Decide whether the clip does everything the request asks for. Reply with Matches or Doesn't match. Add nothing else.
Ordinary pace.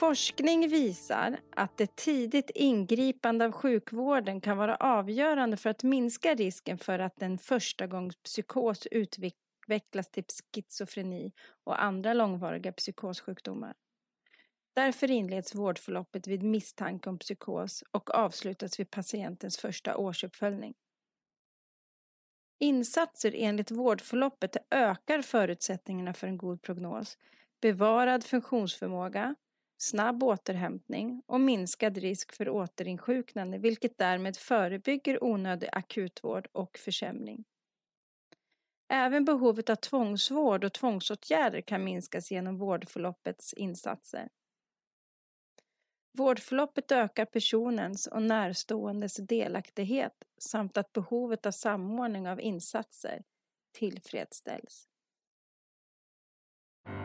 Doesn't match